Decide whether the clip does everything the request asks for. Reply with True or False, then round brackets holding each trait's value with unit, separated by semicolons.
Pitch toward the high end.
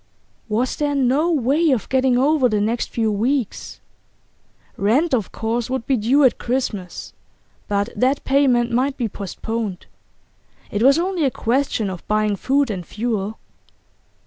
True (245 Hz)